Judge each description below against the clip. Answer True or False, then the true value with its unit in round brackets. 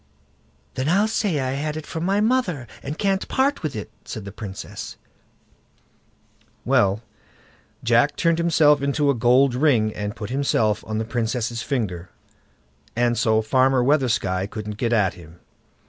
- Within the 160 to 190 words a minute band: False (150 wpm)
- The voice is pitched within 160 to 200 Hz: False (125 Hz)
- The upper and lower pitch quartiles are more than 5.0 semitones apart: True (5.6 semitones)